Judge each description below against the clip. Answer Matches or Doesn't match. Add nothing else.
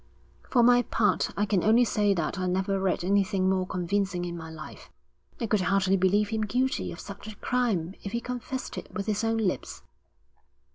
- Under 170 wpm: Doesn't match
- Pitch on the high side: Matches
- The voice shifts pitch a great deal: Doesn't match